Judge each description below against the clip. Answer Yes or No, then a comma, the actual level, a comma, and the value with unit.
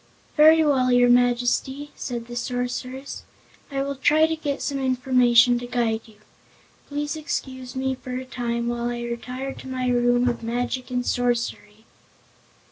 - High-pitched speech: Yes, very high, 250 Hz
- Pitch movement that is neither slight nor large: No, narrow, 1.7 semitones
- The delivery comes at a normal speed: Yes, average, 155 wpm